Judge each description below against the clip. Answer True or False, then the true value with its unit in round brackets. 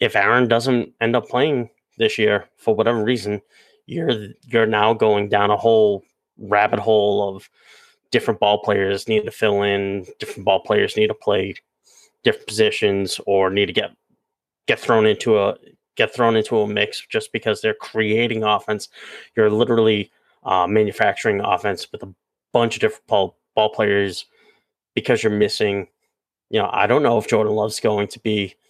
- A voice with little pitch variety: True (2.2 semitones)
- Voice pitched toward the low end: True (110 Hz)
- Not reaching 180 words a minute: True (170 wpm)